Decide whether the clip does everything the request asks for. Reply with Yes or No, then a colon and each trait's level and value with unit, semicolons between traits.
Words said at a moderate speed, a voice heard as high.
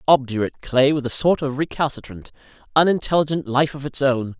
No: average, 165 wpm; medium, 140 Hz